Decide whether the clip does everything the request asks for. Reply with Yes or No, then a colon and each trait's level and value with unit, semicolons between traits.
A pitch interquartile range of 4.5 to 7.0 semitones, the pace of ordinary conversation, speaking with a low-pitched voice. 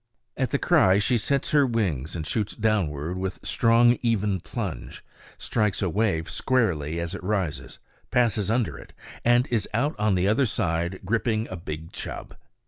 Yes: average, 5.0 semitones; average, 165 wpm; low, 105 Hz